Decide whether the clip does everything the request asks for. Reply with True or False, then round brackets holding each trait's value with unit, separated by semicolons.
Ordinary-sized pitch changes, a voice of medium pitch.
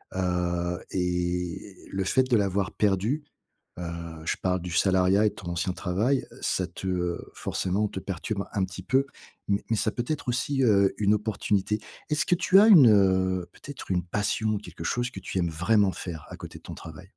False (3.4 semitones; 95 Hz)